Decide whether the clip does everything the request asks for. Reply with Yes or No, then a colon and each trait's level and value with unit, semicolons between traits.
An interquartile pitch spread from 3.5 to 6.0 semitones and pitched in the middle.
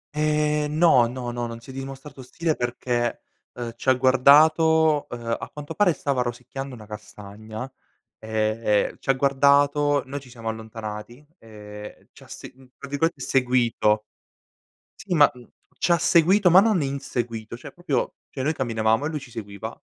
No: average, 4.4 semitones; low, 130 Hz